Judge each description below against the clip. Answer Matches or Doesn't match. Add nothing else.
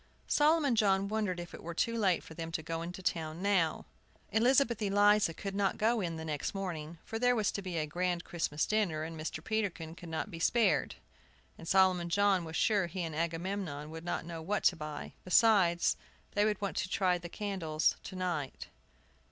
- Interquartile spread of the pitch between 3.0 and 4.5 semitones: Matches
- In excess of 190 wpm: Matches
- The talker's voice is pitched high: Doesn't match